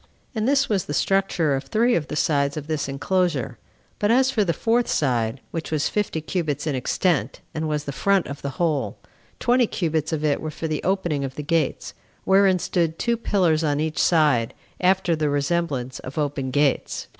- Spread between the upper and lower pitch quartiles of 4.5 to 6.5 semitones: Yes, average, 4.8 semitones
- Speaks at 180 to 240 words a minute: Yes, average, 195 wpm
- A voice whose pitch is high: No, medium, 155 Hz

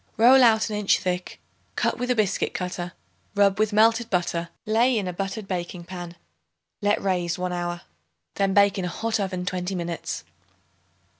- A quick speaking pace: No, average, 170 wpm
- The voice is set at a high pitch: Yes, high, 195 Hz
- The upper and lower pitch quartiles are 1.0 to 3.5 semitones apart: Yes, average, 3.2 semitones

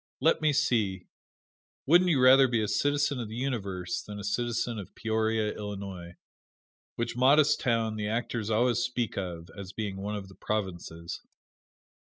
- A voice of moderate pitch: No, low, 110 Hz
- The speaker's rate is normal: Yes, average, 160 wpm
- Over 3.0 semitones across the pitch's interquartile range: Yes, average, 3.9 semitones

